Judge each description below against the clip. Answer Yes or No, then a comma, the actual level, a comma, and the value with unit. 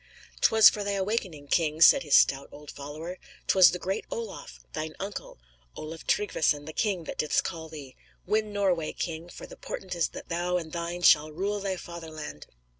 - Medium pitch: Yes, medium, 170 Hz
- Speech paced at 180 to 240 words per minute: Yes, average, 185 wpm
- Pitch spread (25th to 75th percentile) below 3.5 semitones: No, average, 3.8 semitones